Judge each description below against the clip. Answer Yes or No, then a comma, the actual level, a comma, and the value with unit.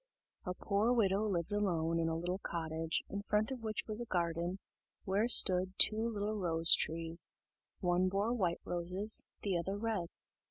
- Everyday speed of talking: Yes, average, 165 wpm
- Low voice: No, high, 190 Hz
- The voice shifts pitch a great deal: No, average, 3.8 semitones